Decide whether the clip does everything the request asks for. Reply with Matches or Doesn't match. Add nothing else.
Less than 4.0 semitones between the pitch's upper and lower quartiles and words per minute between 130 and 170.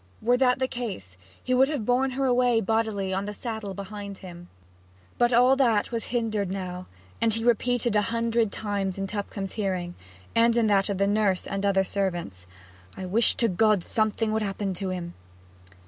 Doesn't match